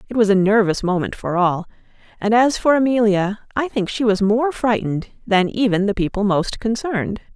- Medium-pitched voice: No, high, 215 Hz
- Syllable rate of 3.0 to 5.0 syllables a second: No, 5.3 syllables/s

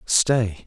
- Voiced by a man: Yes, male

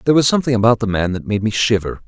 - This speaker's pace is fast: Yes, fast, 290 wpm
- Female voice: No, male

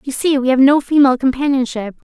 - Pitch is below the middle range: No, very high, 270 Hz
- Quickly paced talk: No, average, 195 wpm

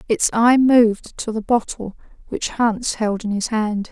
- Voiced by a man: No, female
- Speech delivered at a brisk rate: No, average, 185 wpm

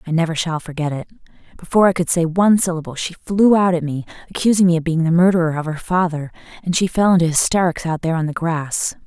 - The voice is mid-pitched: Yes, medium, 170 Hz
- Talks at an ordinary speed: No, fast, 230 wpm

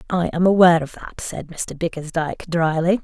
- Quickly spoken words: No, average, 180 wpm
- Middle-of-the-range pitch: Yes, medium, 170 Hz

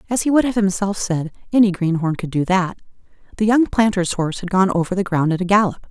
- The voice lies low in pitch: No, high, 190 Hz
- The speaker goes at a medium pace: No, fast, 235 wpm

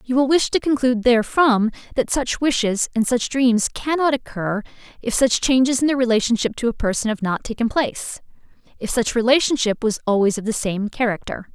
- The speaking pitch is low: No, high, 240 Hz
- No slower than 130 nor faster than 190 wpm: Yes, average, 185 wpm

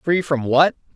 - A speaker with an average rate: Yes, average, 190 wpm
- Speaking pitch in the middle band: Yes, medium, 150 Hz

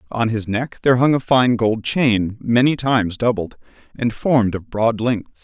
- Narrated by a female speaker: No, male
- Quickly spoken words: No, average, 190 wpm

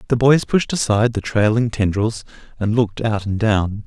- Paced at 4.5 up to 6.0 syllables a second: Yes, 5.1 syllables/s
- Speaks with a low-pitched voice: Yes, low, 110 Hz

